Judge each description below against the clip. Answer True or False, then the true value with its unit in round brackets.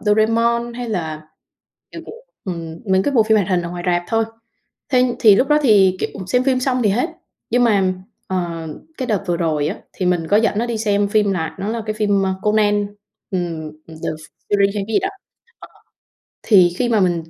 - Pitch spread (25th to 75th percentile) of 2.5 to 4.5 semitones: True (4.1 semitones)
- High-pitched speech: True (205 Hz)